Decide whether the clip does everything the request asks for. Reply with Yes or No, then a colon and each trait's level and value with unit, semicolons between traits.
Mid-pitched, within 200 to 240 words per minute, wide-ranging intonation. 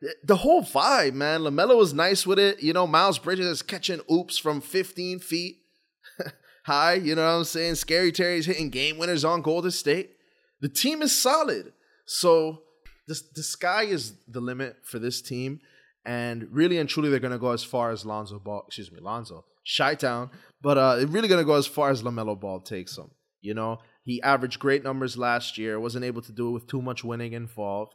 Yes: medium, 145 Hz; fast, 205 wpm; wide, 6.0 semitones